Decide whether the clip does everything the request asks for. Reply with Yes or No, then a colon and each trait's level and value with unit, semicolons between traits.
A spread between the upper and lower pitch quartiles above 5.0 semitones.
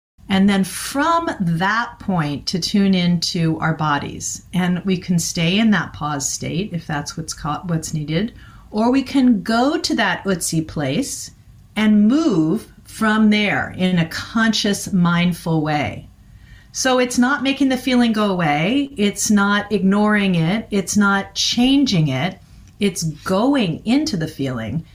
Yes: wide, 5.4 semitones